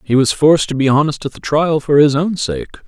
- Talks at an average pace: No, fast, 270 wpm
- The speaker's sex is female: No, male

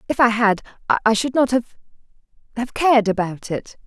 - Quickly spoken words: No, average, 155 wpm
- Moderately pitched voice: No, high, 230 Hz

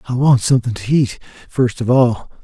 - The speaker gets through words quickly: No, average, 195 wpm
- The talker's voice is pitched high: No, low, 120 Hz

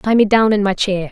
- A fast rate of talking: Yes, fast, 325 wpm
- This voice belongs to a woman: Yes, female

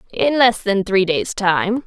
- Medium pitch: No, high, 200 Hz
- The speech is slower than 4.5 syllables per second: Yes, 4.3 syllables/s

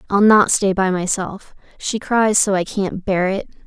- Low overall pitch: No, high, 195 Hz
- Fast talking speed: No, average, 195 wpm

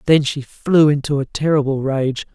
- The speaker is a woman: No, male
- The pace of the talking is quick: No, average, 180 wpm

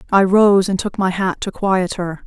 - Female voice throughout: Yes, female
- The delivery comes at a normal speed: No, fast, 240 wpm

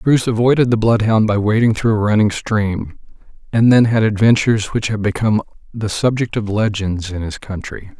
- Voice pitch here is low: Yes, low, 110 Hz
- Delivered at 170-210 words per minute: Yes, average, 180 wpm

